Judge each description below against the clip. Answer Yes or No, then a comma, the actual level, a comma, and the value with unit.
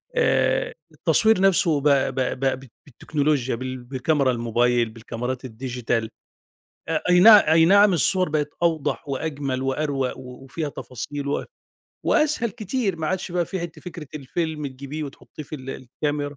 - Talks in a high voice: No, medium, 145 Hz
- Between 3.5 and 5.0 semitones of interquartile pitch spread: Yes, average, 4.4 semitones